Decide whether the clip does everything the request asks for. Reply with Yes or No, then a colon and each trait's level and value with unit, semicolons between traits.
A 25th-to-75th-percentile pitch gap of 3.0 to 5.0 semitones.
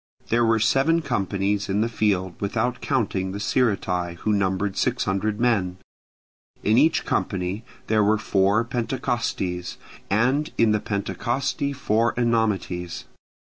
Yes: average, 3.6 semitones